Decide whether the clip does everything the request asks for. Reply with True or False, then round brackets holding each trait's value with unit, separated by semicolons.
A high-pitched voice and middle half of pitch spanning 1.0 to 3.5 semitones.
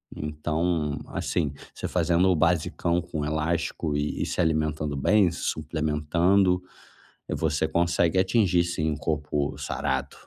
False (80 Hz; 2.4 semitones)